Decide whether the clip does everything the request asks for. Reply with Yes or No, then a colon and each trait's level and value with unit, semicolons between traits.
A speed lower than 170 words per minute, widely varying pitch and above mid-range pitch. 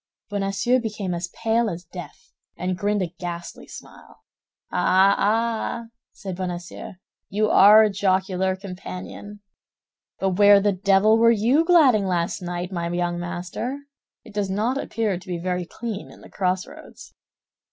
No: average, 145 wpm; average, 3.0 semitones; high, 195 Hz